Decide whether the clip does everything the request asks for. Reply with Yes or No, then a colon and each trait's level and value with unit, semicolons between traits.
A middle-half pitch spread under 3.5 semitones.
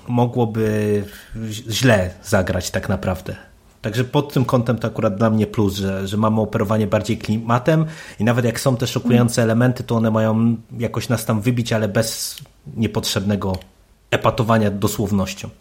Yes: narrow, 2.4 semitones